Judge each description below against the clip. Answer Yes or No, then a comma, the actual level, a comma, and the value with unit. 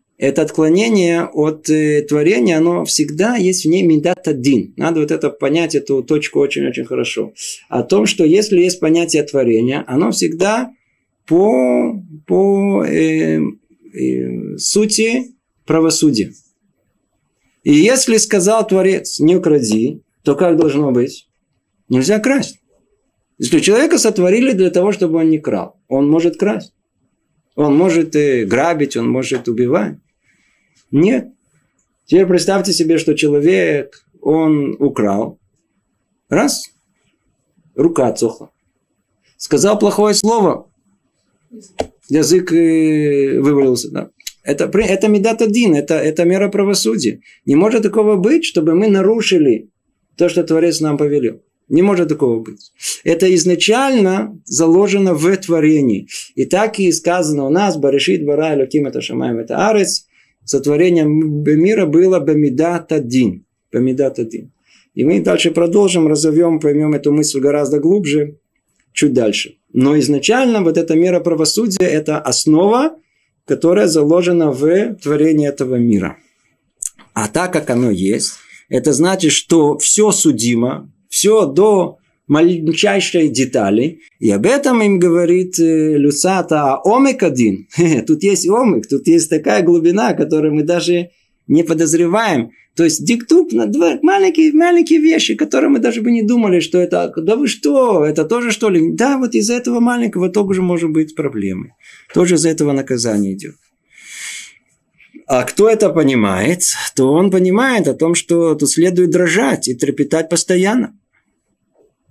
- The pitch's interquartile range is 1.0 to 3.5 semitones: No, average, 5.2 semitones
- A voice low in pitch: No, medium, 170 Hz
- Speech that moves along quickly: No, average, 130 wpm